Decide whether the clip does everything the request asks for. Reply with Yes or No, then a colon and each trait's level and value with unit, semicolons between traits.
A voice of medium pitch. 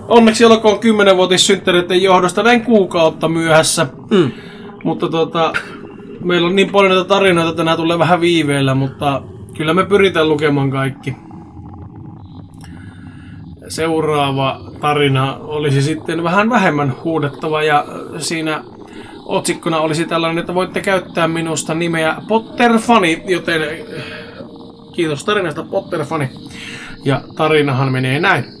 Yes: medium, 160 Hz